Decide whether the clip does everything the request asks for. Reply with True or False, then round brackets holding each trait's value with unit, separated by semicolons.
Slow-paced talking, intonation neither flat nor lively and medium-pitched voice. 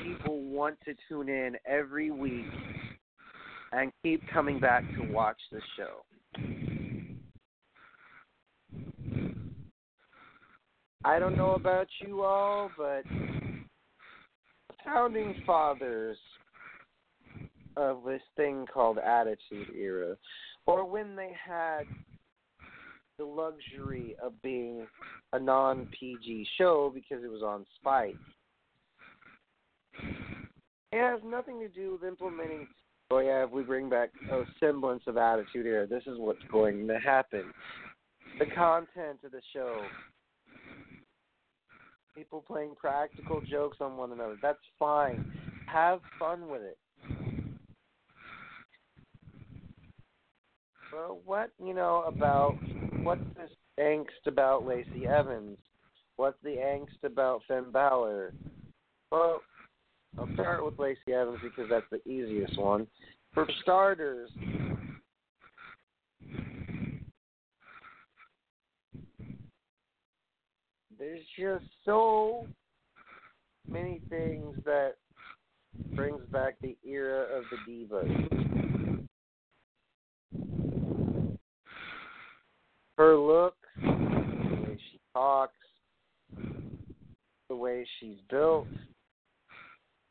False (95 wpm; 6.3 semitones; 150 Hz)